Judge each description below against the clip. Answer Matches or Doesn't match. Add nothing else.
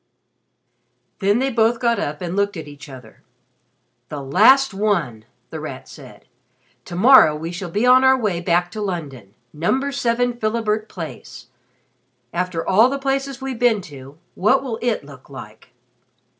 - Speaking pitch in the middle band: Doesn't match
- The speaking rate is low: Doesn't match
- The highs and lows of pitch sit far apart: Matches